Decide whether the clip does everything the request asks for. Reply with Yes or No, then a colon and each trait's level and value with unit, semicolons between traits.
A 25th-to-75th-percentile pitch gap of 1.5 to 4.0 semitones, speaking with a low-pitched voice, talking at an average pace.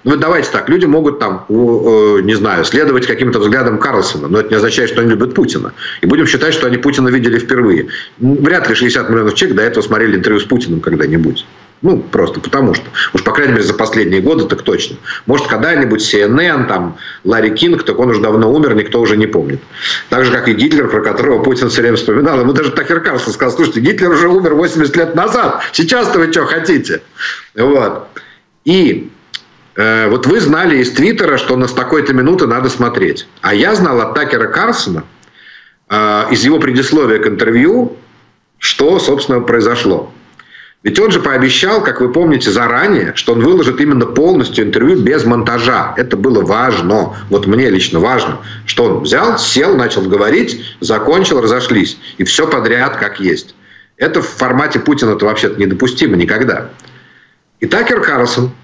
No: average, 3.4 semitones; low, 120 Hz; fast, 175 wpm